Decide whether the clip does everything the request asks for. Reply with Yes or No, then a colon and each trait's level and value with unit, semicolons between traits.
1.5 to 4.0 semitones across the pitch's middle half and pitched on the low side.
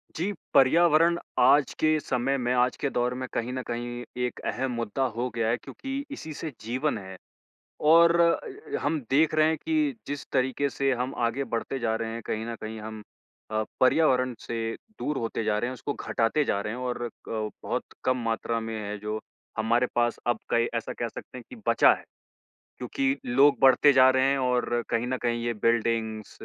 Yes: average, 3.6 semitones; low, 125 Hz